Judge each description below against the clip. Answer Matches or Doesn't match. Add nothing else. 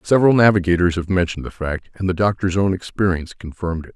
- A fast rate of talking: Doesn't match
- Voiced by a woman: Doesn't match